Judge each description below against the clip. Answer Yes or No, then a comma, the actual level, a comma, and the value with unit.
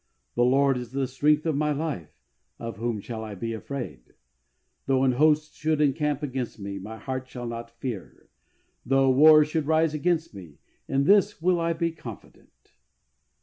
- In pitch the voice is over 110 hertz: Yes, low, 135 Hz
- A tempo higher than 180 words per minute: No, average, 170 wpm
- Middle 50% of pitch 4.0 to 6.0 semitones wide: Yes, average, 4.6 semitones